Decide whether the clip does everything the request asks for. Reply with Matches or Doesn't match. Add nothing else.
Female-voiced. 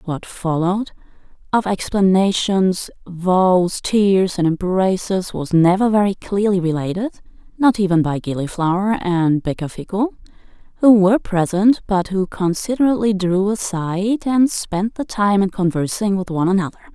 Matches